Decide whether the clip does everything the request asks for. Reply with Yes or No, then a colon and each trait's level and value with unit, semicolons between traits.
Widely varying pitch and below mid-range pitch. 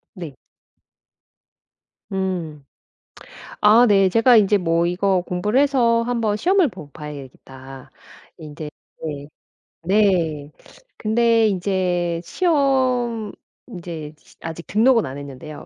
No: wide, 6.5 semitones; high, 190 Hz